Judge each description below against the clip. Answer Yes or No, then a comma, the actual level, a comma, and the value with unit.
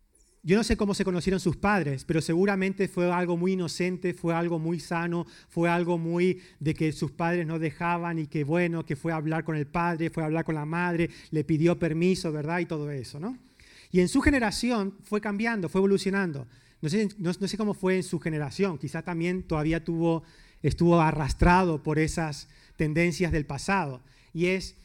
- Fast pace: Yes, fast, 200 wpm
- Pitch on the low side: No, medium, 170 Hz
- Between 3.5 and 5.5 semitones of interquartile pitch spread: No, narrow, 2.6 semitones